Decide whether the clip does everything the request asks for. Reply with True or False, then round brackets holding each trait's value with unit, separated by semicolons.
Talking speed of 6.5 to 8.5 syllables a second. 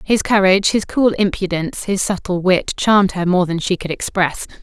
False (5.3 syllables/s)